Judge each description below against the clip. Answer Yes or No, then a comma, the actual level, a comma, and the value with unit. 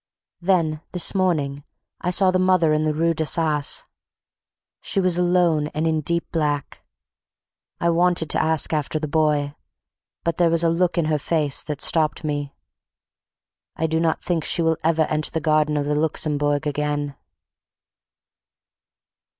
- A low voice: No, medium, 160 Hz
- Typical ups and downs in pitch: No, narrow, 2.1 semitones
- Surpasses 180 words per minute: No, average, 155 wpm